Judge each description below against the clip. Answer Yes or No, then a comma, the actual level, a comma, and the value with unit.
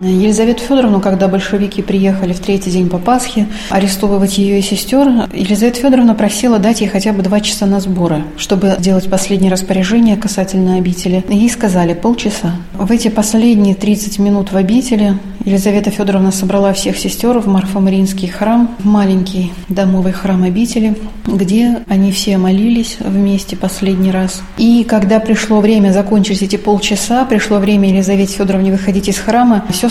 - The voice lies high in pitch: Yes, high, 200 Hz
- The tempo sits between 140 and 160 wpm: Yes, average, 155 wpm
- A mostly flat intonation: Yes, narrow, 2.1 semitones